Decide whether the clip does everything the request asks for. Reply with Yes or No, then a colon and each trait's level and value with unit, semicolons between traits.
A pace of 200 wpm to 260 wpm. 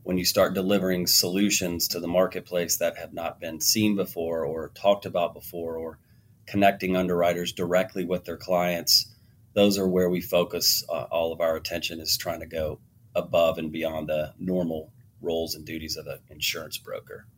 No: average, 175 wpm